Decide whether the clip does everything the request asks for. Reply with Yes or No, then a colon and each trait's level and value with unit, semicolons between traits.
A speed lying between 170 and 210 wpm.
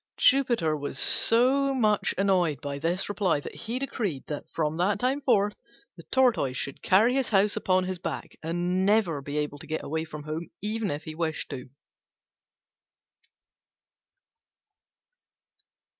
No: average, 145 wpm